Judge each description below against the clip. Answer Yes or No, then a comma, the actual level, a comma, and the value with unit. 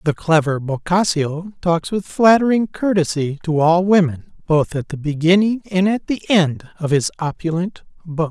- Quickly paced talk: No, average, 160 wpm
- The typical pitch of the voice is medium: Yes, medium, 170 Hz